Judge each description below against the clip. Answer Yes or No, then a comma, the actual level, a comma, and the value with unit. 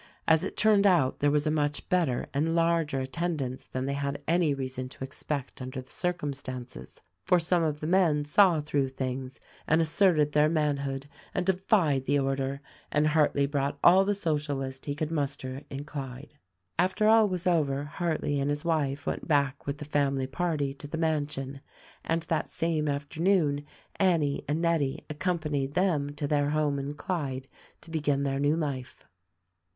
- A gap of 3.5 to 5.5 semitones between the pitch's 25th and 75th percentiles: No, average, 3.0 semitones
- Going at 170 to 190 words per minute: Yes, average, 175 wpm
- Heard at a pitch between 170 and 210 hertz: No, medium, 145 Hz